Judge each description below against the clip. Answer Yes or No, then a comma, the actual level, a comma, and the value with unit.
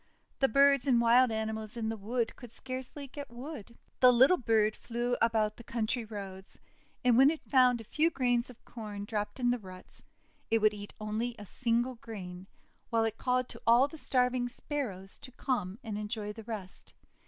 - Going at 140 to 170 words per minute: No, average, 190 wpm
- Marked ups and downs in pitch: No, average, 2.9 semitones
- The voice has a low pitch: No, high, 235 Hz